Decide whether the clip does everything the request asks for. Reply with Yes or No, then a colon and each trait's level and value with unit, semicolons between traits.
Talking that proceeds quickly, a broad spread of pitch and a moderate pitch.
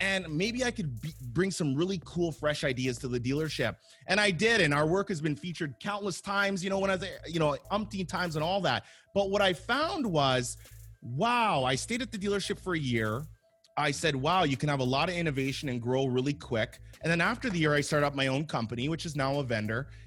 Yes: fast, 240 wpm; wide, 6.4 semitones; medium, 155 Hz